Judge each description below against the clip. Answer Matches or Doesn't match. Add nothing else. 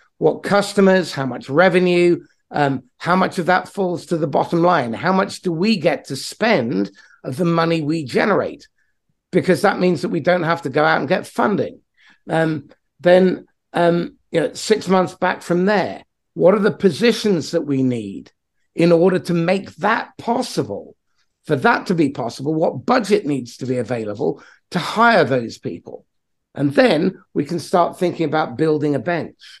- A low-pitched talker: Doesn't match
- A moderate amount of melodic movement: Matches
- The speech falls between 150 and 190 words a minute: Matches